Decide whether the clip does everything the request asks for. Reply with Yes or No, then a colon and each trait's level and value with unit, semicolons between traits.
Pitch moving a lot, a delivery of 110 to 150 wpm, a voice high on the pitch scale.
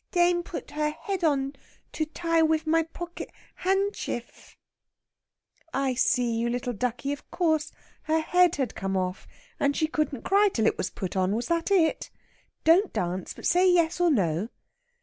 No: wide, 6.2 semitones; average, 170 wpm; very high, 310 Hz